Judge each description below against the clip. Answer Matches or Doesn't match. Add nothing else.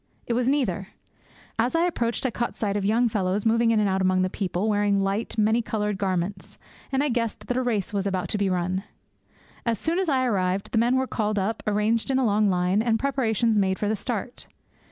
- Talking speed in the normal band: Doesn't match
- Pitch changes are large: Doesn't match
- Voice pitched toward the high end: Matches